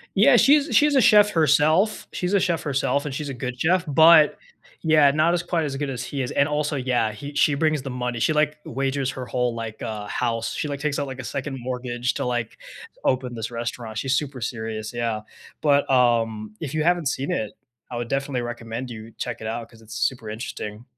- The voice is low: Yes, low, 130 Hz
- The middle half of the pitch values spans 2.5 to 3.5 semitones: No, average, 4.2 semitones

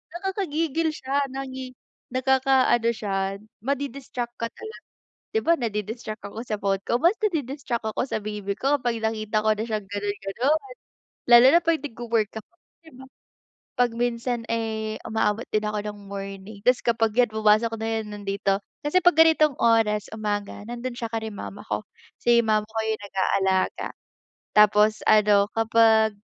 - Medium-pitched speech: No, high, 225 Hz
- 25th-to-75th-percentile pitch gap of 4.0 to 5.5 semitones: No, average, 3.4 semitones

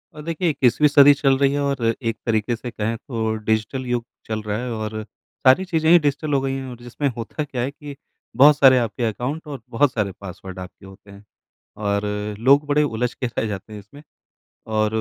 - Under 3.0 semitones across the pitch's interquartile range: No, average, 4.7 semitones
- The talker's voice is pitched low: Yes, low, 125 Hz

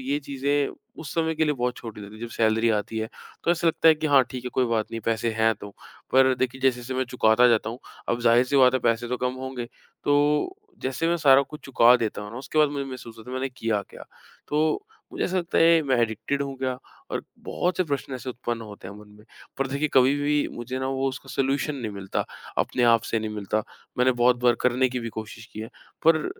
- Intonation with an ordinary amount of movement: Yes, average, 3.4 semitones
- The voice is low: Yes, low, 130 Hz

